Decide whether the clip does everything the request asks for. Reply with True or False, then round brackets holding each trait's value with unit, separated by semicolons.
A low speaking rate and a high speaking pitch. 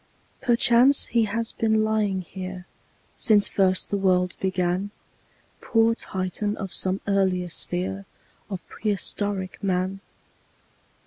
True (110 wpm; 195 Hz)